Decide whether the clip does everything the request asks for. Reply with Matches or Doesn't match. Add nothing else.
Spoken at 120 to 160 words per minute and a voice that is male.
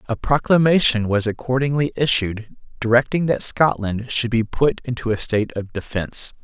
Matches